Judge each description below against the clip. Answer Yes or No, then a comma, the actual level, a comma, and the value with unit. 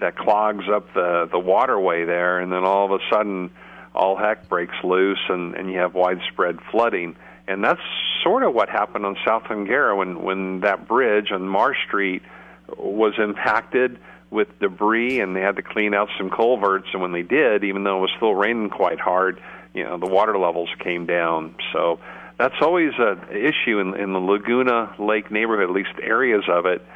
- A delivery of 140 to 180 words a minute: No, average, 190 wpm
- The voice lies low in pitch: Yes, low, 100 Hz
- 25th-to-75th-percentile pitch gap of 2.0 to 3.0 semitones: Yes, narrow, 2.4 semitones